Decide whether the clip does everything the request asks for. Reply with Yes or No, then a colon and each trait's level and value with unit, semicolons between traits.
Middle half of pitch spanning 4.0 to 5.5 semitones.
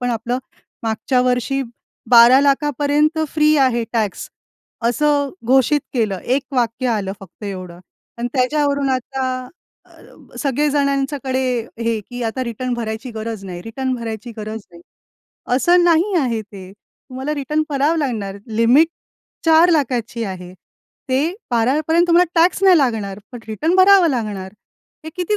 Yes: average, 4.7 semitones